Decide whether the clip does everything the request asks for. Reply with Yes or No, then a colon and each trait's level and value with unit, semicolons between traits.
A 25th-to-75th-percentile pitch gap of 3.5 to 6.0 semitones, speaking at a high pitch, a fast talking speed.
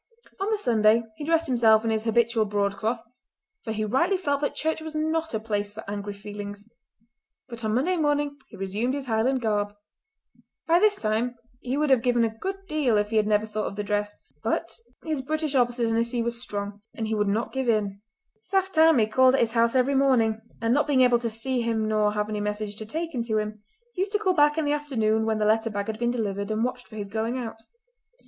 Yes: average, 4.3 semitones; high, 230 Hz; fast, 225 wpm